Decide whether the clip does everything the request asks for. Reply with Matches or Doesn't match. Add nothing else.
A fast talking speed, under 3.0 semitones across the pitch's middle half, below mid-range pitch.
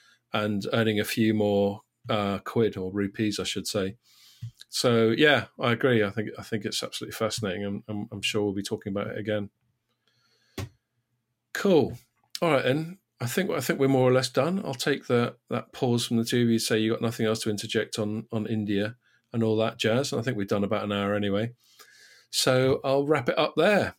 Matches